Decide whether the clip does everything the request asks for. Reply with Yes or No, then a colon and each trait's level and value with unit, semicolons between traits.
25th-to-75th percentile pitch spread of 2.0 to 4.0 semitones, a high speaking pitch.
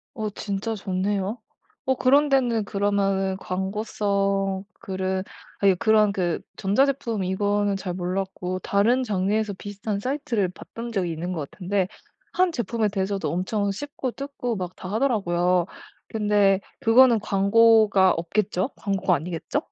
Yes: average, 2.9 semitones; high, 200 Hz